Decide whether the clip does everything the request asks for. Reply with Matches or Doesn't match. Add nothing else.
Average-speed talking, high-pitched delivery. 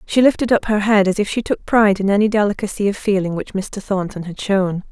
Doesn't match